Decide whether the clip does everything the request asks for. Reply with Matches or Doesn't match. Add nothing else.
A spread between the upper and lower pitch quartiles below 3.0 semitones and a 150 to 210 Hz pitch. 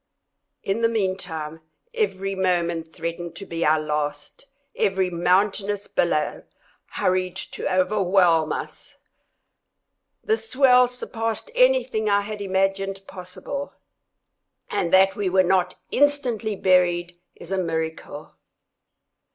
Doesn't match